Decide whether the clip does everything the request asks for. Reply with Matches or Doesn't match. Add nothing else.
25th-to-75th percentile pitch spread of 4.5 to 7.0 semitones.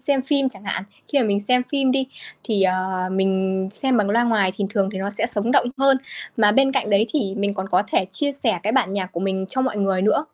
Matches